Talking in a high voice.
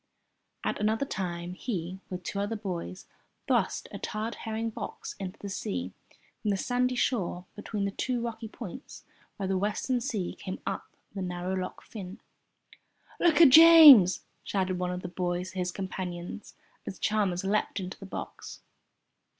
Yes: high, 195 Hz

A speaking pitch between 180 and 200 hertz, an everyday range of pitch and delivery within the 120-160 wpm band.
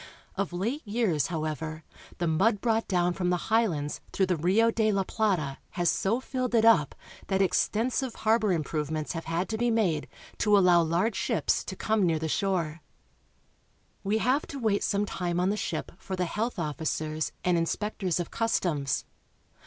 No: medium, 185 Hz; average, 4.9 semitones; average, 175 wpm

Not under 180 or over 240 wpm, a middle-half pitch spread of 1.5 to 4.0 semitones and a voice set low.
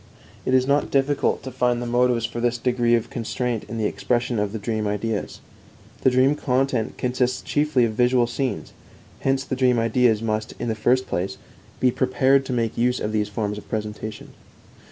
Yes: average, 185 wpm; average, 2.7 semitones; low, 120 Hz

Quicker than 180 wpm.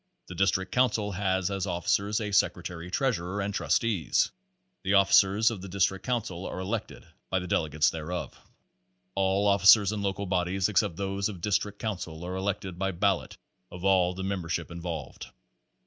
No: average, 170 wpm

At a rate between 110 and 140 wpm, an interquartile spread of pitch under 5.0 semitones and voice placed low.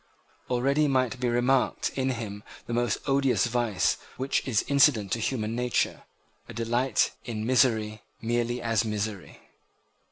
Yes: slow, 135 wpm; average, 2.8 semitones; low, 120 Hz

